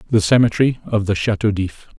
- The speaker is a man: Yes, male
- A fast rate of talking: No, average, 180 wpm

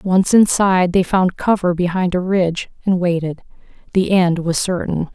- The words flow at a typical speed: Yes, average, 165 wpm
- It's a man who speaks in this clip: No, female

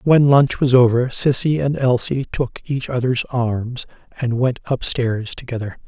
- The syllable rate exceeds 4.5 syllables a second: No, 4.2 syllables/s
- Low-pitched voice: Yes, low, 125 Hz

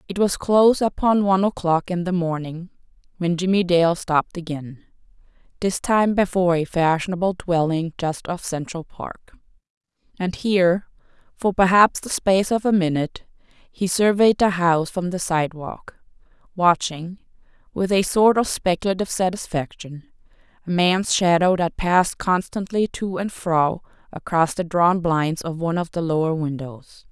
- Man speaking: No, female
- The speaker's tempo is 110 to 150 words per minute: Yes, average, 140 wpm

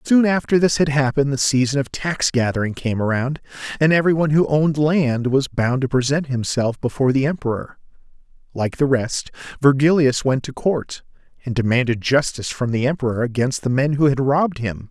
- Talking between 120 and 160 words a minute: No, average, 180 wpm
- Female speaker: No, male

